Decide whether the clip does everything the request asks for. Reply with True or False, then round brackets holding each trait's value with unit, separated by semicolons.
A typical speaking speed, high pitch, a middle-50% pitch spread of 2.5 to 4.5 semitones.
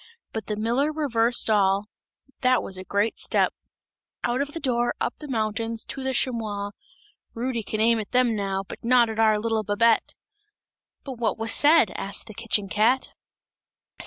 True (170 wpm; 225 Hz; 2.8 semitones)